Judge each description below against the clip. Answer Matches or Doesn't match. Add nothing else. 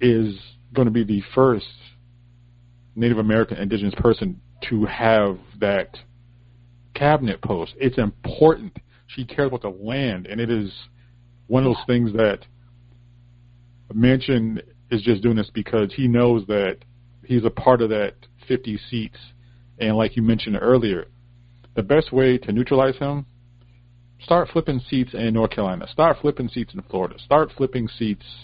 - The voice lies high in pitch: Doesn't match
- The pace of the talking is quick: Doesn't match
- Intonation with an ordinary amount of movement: Doesn't match